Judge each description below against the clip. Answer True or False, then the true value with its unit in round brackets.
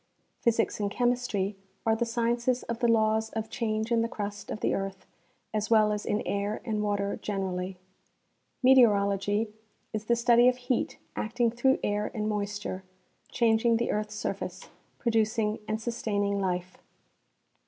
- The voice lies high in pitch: True (215 Hz)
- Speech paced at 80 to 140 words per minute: False (150 wpm)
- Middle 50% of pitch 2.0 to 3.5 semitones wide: True (2.4 semitones)